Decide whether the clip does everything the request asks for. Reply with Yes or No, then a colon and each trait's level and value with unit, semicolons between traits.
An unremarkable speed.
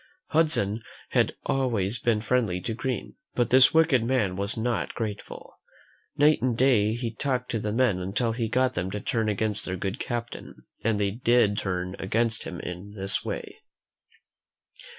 Yes: average, 165 wpm